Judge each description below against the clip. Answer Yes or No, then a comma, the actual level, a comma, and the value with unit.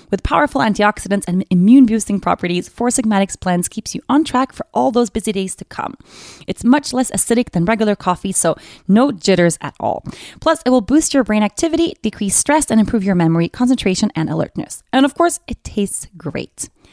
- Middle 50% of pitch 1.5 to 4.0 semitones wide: No, average, 5.2 semitones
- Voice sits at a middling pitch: No, high, 220 Hz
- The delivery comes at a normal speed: Yes, average, 195 wpm